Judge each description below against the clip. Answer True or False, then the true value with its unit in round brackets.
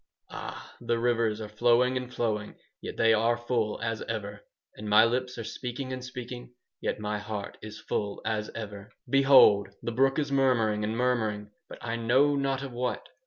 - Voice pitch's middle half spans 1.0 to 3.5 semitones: True (3.0 semitones)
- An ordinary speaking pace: True (180 wpm)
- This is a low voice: True (115 Hz)